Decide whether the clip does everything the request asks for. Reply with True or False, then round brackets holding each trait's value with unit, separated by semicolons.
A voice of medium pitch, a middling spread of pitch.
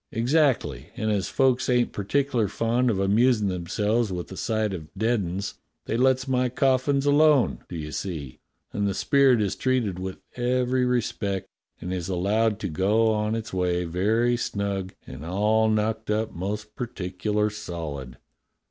False (105 Hz; 4.5 semitones)